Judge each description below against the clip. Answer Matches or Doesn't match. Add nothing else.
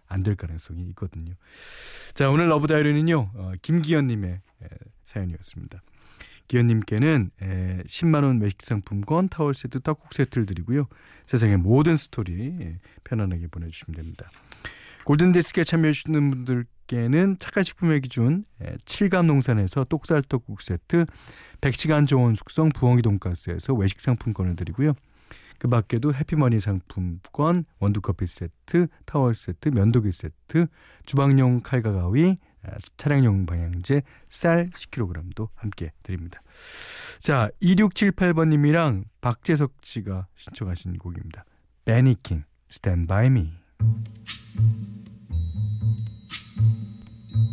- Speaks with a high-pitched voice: Doesn't match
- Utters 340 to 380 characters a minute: Doesn't match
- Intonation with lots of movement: Matches